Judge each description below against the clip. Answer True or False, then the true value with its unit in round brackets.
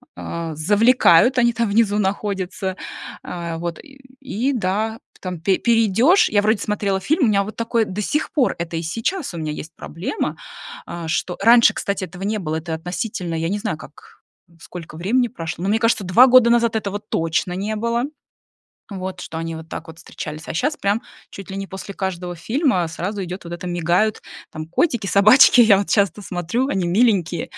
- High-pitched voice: True (195 Hz)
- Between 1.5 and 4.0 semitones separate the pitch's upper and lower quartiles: False (4.7 semitones)